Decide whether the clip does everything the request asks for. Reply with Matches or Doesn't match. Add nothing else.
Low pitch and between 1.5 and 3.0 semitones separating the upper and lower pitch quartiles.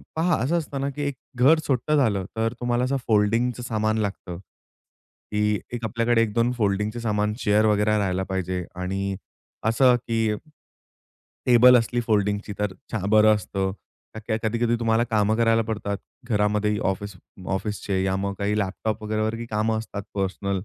Matches